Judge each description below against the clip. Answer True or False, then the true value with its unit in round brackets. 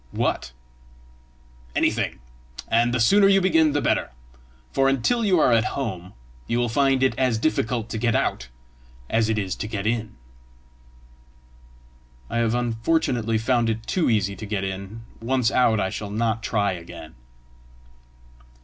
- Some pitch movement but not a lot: True (3.3 semitones)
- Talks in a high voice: False (115 Hz)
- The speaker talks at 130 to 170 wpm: True (150 wpm)